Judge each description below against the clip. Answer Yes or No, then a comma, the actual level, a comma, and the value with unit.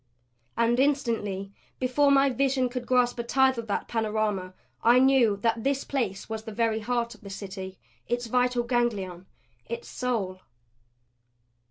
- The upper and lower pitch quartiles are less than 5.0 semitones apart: Yes, average, 3.2 semitones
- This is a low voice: No, high, 235 Hz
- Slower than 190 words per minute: Yes, average, 150 wpm